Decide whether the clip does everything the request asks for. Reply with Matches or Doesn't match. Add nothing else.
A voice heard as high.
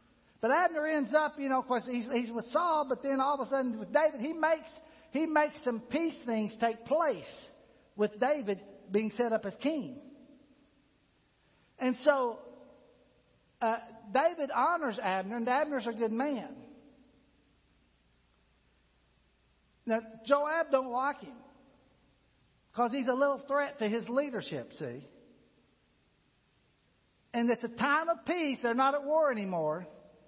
Matches